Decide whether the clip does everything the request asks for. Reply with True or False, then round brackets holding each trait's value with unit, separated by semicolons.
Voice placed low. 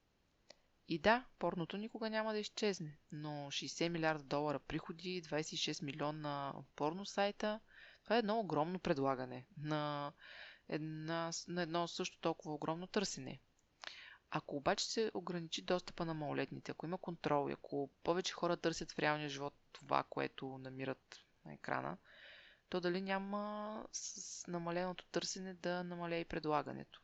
False (170 Hz)